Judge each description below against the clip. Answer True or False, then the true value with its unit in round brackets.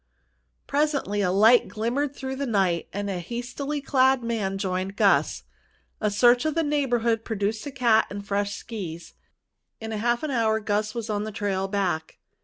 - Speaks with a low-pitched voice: False (220 Hz)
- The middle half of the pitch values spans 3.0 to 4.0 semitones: True (3.7 semitones)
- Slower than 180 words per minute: True (170 wpm)